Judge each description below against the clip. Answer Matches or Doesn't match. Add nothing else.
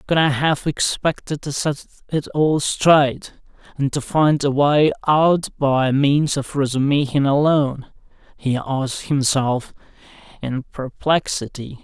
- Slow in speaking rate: Matches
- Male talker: Matches